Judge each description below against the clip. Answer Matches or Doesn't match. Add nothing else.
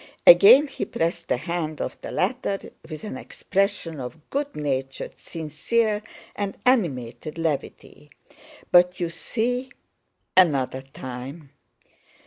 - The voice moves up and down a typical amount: Doesn't match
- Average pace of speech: Doesn't match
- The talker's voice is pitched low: Doesn't match